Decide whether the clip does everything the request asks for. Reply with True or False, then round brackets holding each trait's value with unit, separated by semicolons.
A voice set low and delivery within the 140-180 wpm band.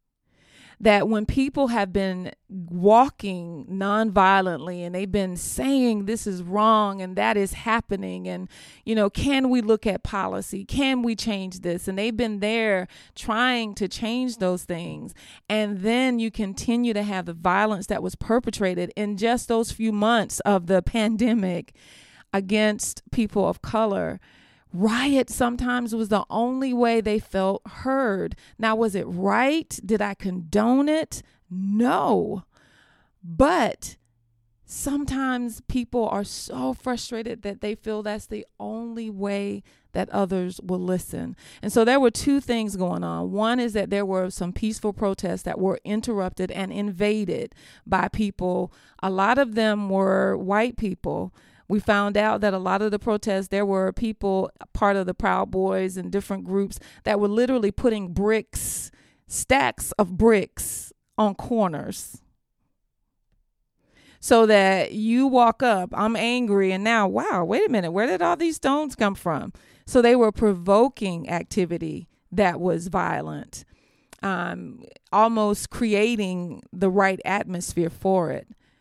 False (205 Hz; 145 wpm)